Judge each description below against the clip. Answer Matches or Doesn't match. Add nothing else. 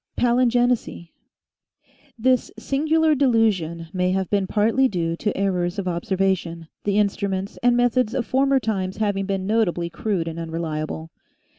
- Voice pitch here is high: Matches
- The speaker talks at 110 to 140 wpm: Matches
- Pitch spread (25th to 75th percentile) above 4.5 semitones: Matches